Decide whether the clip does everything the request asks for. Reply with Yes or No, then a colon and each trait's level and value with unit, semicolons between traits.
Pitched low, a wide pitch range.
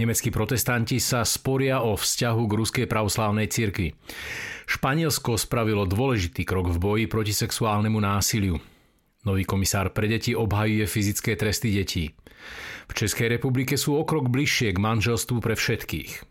No: low, 110 Hz; average, 2.8 semitones